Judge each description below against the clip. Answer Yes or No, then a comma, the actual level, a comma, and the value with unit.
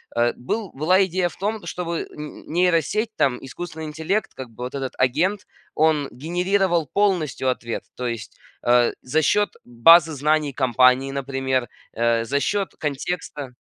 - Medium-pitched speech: Yes, medium, 150 Hz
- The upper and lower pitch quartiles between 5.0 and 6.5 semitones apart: Yes, wide, 5.6 semitones